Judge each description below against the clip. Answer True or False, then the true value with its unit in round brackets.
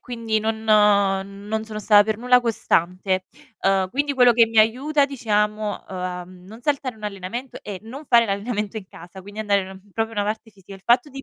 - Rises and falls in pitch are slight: False (3.1 semitones)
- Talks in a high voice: True (215 Hz)